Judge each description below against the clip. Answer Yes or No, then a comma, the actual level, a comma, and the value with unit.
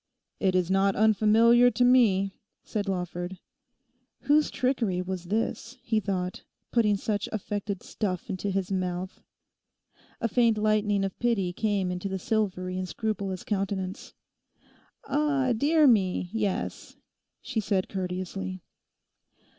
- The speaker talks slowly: Yes, slow, 125 wpm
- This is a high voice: Yes, high, 200 Hz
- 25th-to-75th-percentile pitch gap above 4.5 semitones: No, average, 3.2 semitones